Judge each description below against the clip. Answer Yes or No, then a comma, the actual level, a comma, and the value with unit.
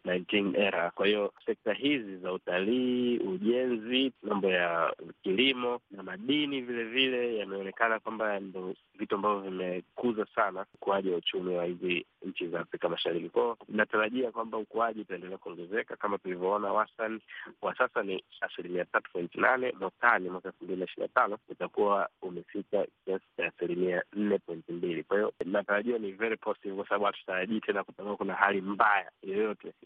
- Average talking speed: No, fast, 150 wpm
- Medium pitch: No, low, 105 Hz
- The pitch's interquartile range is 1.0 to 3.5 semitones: No, average, 4.1 semitones